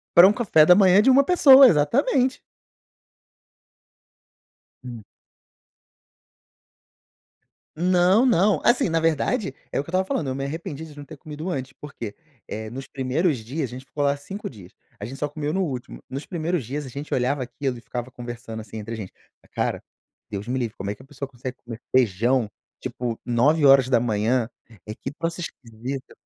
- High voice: No, low, 135 Hz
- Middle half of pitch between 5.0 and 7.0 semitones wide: Yes, wide, 5.5 semitones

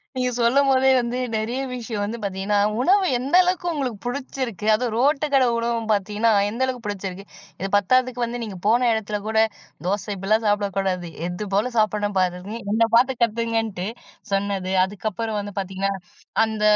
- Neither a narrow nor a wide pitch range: Yes, average, 3.6 semitones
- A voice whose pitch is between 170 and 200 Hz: No, high, 220 Hz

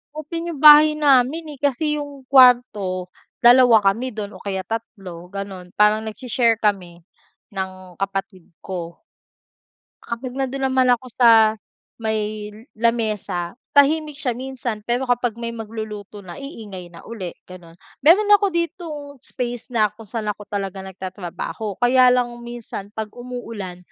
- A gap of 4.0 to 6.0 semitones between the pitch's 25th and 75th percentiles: Yes, average, 4.7 semitones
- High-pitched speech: Yes, high, 230 Hz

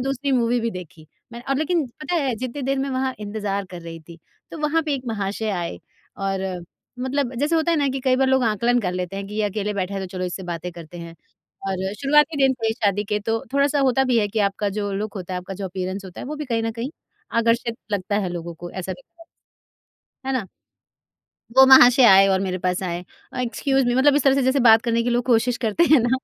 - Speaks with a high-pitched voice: Yes, high, 225 Hz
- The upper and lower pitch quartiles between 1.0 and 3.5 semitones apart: No, wide, 5.5 semitones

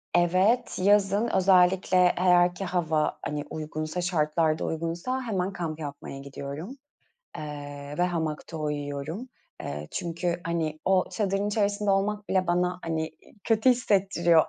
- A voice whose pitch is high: No, medium, 175 Hz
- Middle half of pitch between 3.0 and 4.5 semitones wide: Yes, average, 3.9 semitones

